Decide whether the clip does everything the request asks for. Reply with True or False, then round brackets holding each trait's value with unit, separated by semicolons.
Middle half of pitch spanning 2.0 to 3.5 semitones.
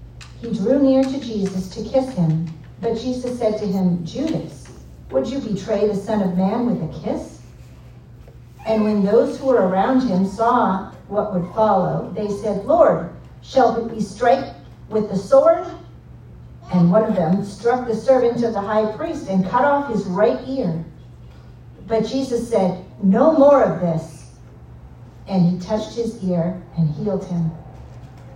False (4.8 semitones)